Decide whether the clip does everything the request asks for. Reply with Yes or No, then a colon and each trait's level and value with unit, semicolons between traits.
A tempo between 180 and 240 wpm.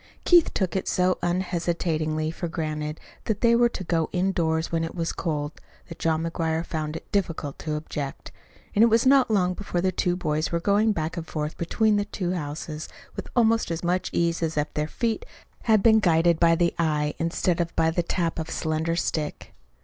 Yes: fast, 205 wpm